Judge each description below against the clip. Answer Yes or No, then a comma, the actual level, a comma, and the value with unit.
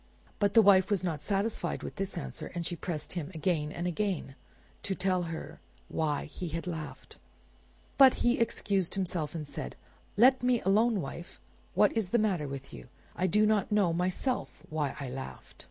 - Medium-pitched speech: Yes, medium, 180 Hz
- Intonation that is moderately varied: Yes, average, 4.5 semitones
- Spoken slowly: No, average, 180 wpm